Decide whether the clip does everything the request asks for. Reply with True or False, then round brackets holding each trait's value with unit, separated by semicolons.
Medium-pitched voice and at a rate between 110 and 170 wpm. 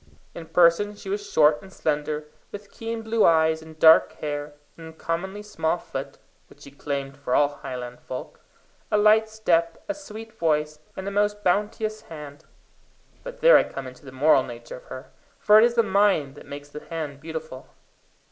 False (160 Hz; 185 wpm)